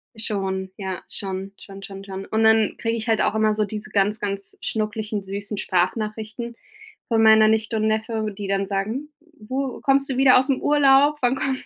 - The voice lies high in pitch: Yes, high, 215 Hz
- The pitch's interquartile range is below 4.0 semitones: Yes, average, 2.9 semitones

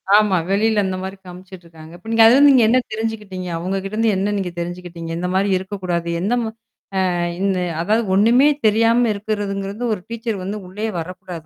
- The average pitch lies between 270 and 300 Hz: No, high, 195 Hz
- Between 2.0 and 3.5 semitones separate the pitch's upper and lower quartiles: Yes, average, 3.2 semitones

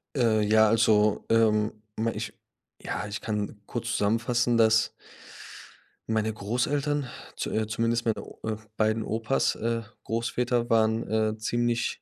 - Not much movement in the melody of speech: Yes, narrow, 1.3 semitones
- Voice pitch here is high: No, low, 110 Hz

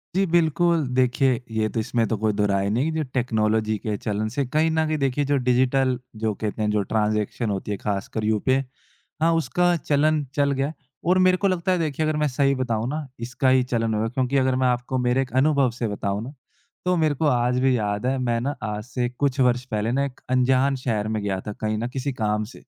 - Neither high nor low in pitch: No, low, 125 Hz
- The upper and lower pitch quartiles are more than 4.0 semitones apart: Yes, average, 4.5 semitones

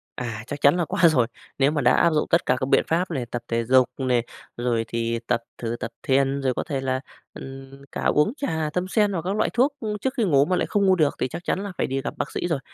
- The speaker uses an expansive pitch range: Yes, wide, 5.9 semitones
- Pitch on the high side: No, medium, 140 Hz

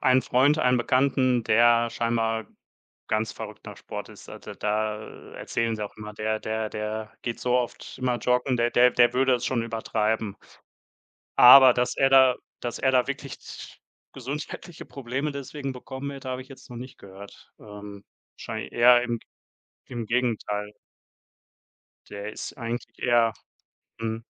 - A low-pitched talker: Yes, low, 120 Hz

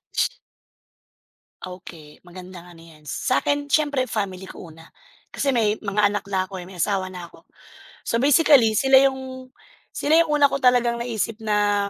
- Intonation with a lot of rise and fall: Yes, wide, 6.0 semitones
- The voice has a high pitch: Yes, high, 210 Hz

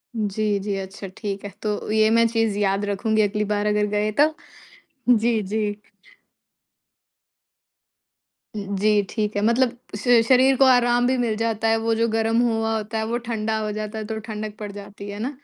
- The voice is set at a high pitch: Yes, high, 215 Hz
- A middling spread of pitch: No, narrow, 1.7 semitones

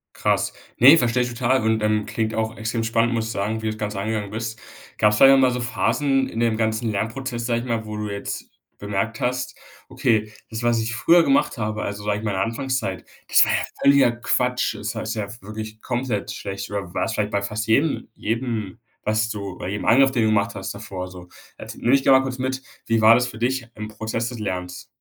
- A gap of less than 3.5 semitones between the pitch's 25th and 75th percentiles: Yes, narrow, 2.5 semitones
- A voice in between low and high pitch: No, low, 110 Hz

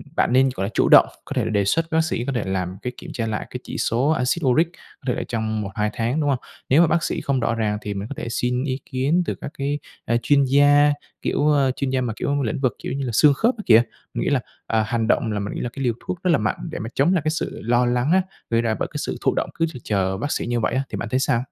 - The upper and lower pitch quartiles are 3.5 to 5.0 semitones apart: Yes, average, 4.2 semitones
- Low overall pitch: Yes, low, 125 Hz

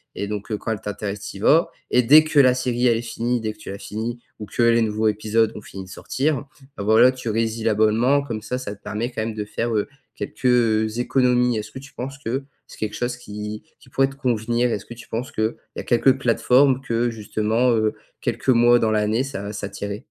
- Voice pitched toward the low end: Yes, low, 115 Hz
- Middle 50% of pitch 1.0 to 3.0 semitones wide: Yes, narrow, 2.5 semitones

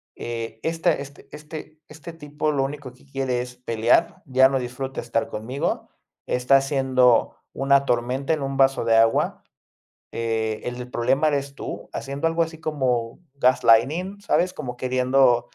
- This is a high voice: No, low, 135 Hz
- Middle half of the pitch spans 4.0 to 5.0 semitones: No, average, 3.1 semitones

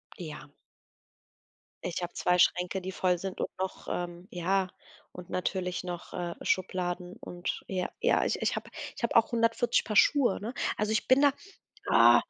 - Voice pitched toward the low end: No, medium, 185 Hz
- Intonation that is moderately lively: Yes, average, 3.1 semitones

